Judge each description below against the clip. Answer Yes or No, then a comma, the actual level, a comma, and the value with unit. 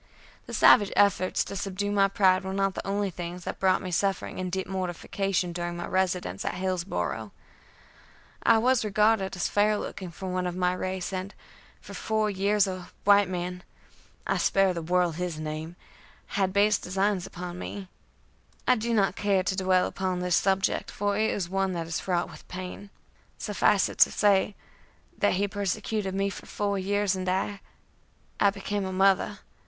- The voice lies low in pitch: No, high, 190 Hz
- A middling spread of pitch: No, narrow, 1.9 semitones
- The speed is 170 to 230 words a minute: Yes, average, 180 wpm